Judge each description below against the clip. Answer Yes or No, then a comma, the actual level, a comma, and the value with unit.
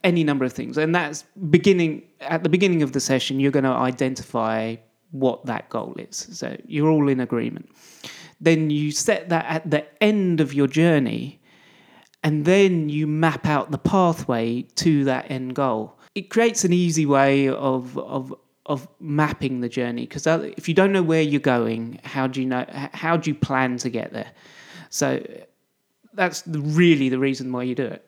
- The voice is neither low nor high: Yes, medium, 150 Hz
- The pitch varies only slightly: No, average, 4.0 semitones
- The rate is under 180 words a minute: No, average, 185 wpm